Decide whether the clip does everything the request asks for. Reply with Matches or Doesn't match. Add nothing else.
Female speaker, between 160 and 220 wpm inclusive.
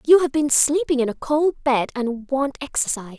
Matches